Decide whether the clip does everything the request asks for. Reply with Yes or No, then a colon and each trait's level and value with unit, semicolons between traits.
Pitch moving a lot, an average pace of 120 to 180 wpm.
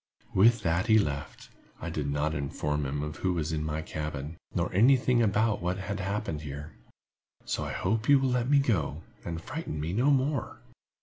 No: wide, 7.2 semitones; average, 195 wpm